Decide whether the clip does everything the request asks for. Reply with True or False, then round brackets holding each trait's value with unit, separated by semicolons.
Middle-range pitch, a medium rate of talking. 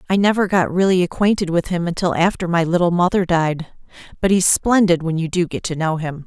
False (175 Hz; 220 wpm)